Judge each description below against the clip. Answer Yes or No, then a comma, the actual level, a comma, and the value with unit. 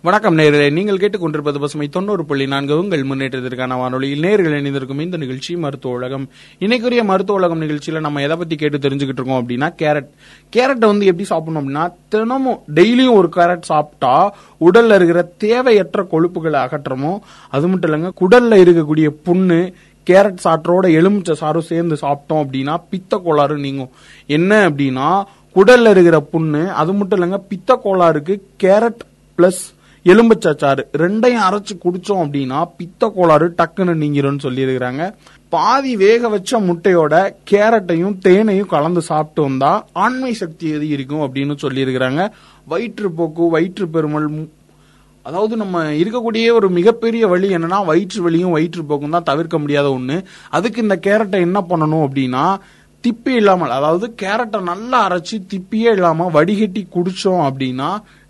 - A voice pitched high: No, medium, 175 Hz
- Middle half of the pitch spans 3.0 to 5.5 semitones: Yes, average, 4.9 semitones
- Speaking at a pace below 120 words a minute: No, fast, 130 wpm